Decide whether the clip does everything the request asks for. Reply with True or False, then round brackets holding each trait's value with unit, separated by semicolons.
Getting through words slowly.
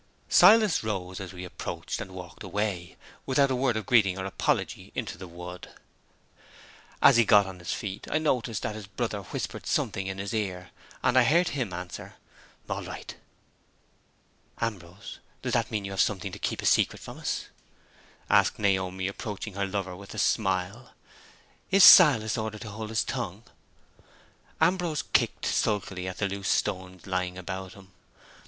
False (165 wpm)